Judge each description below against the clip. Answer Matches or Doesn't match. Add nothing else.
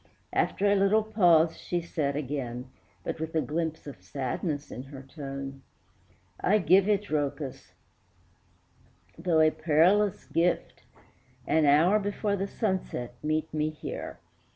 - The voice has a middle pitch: Matches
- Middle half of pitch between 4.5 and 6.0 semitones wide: Matches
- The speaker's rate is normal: Doesn't match